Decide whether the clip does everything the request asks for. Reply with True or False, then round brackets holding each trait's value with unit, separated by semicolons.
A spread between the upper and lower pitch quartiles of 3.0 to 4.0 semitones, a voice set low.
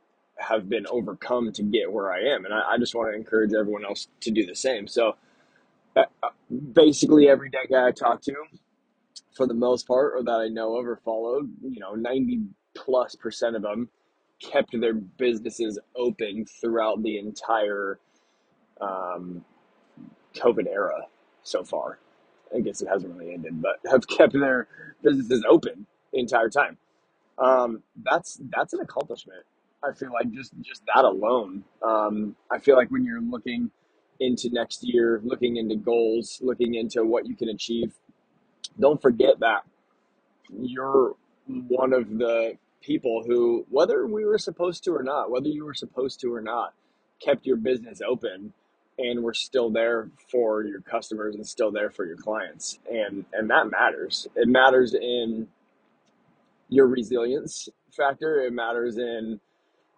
True (3.6 semitones; 120 Hz)